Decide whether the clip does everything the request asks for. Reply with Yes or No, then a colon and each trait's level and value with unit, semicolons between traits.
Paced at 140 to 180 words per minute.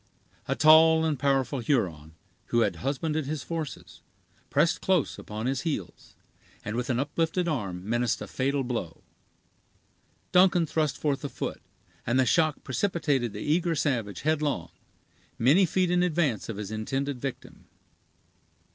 Yes: average, 145 wpm